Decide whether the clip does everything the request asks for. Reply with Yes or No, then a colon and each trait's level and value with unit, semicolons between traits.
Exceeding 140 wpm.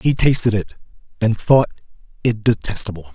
No: slow, 135 wpm